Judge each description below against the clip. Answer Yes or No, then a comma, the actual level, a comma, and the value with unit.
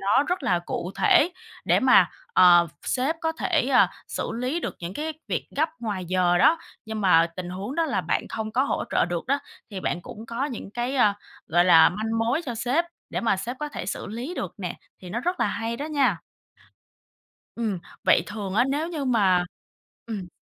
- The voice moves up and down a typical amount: No, wide, 6.8 semitones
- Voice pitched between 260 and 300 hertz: No, high, 225 Hz